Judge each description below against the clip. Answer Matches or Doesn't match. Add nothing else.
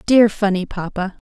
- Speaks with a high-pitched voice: Matches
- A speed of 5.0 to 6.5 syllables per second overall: Doesn't match